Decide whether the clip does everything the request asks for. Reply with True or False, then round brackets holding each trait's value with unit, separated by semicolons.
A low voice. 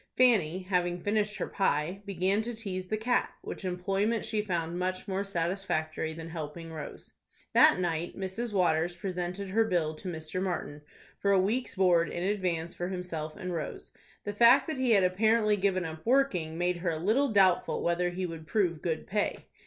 False (185 Hz)